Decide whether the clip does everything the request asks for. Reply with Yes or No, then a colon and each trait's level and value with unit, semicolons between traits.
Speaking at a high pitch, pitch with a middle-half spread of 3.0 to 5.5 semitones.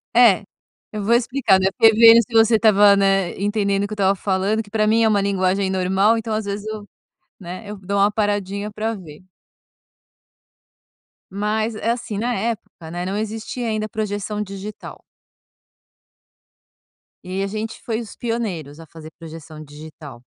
No: high, 205 Hz; narrow, 2.5 semitones